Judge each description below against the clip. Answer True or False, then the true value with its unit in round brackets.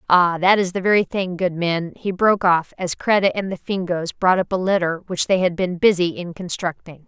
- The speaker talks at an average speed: False (230 wpm)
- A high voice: False (180 Hz)